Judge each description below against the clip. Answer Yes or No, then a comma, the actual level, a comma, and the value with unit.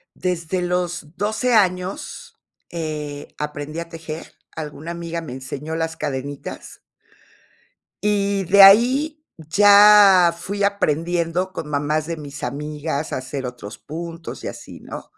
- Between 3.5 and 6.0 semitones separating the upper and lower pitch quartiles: Yes, average, 4.2 semitones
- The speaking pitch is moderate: Yes, medium, 165 Hz